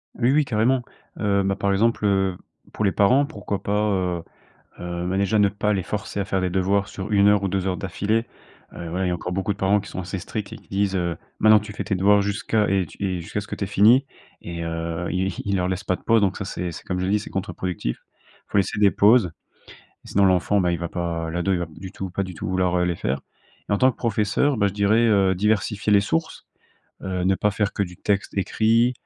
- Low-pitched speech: Yes, low, 100 Hz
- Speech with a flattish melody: Yes, narrow, 2.2 semitones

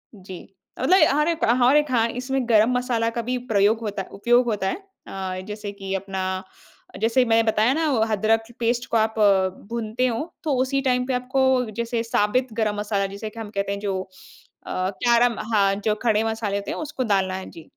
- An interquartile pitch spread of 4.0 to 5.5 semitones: No, average, 3.6 semitones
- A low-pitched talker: No, high, 225 Hz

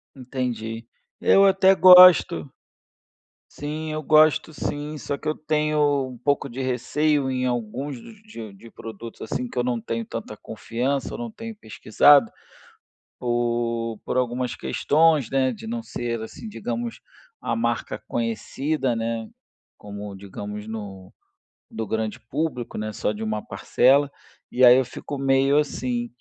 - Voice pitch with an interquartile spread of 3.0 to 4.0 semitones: No, average, 4.4 semitones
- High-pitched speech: No, low, 125 Hz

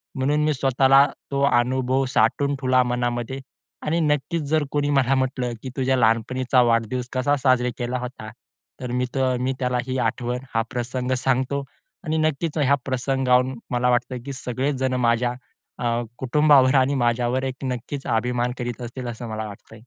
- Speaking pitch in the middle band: No, low, 130 Hz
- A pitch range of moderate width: No, narrow, 1.8 semitones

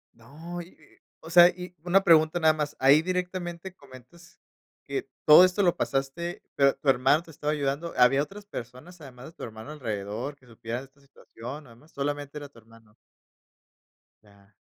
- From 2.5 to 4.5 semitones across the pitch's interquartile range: No, average, 5.3 semitones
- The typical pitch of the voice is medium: Yes, medium, 145 Hz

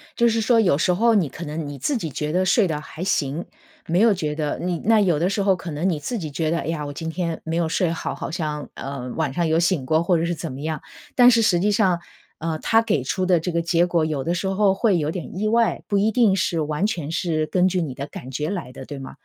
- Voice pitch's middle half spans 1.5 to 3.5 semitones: No, average, 3.9 semitones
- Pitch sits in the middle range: Yes, medium, 170 Hz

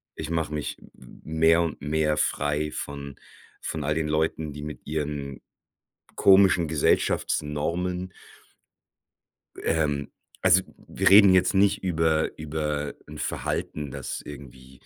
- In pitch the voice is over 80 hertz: No, very low, 75 Hz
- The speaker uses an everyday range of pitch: No, narrow, 2.1 semitones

